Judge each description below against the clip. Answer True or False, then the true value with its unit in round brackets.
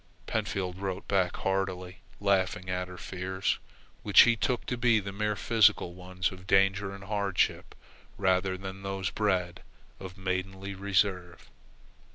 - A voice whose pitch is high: False (95 Hz)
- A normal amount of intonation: False (1.4 semitones)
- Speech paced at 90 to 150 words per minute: True (140 wpm)